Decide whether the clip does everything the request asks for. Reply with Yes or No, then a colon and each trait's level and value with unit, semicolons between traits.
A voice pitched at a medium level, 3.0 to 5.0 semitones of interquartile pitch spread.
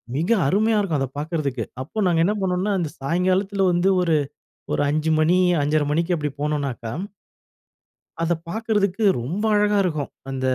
Yes: medium, 170 Hz; average, 4.7 semitones